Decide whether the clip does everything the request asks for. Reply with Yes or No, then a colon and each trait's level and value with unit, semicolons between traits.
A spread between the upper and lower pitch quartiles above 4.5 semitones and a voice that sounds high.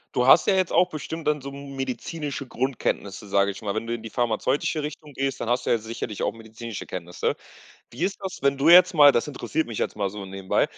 No: average, 5.3 semitones; low, 130 Hz